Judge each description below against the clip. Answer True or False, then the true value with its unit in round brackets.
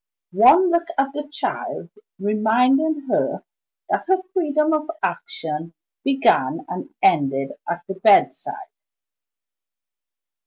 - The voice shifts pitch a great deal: True (8.6 semitones)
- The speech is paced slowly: True (105 wpm)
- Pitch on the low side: False (275 Hz)